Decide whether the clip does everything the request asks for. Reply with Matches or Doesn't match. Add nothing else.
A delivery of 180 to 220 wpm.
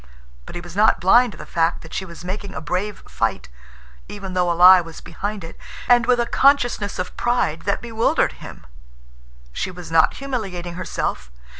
Matches